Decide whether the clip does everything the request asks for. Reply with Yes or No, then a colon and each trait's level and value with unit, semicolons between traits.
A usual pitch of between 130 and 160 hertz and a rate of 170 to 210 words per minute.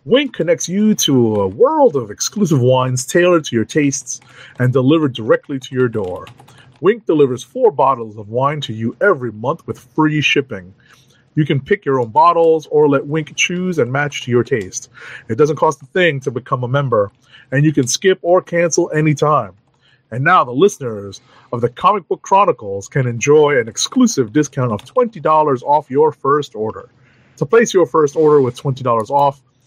Yes: medium, 140 Hz; average, 185 wpm